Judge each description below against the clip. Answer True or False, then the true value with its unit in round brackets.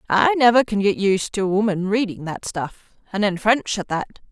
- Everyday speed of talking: False (210 wpm)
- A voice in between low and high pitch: False (205 Hz)